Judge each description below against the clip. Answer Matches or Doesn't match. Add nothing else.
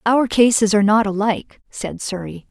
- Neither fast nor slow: Matches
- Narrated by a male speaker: Doesn't match